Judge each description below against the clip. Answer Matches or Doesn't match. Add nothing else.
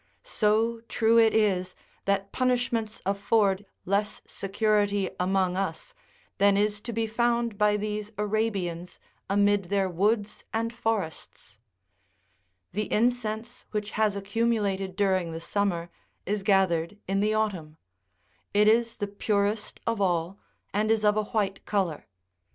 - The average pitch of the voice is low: Doesn't match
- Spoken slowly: Matches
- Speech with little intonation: Matches